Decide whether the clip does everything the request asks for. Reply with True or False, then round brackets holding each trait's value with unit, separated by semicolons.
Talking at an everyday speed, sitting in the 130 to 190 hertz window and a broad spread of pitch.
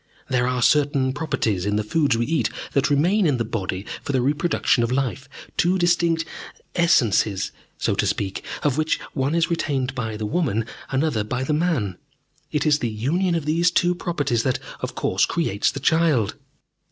True (180 wpm; 140 Hz; 5.7 semitones)